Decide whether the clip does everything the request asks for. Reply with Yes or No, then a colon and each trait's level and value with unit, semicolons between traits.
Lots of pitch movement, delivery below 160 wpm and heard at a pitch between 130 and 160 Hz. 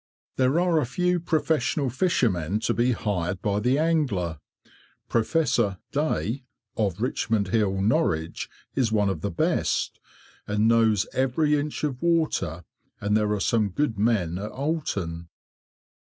No: wide, 6.5 semitones; average, 140 wpm; low, 115 Hz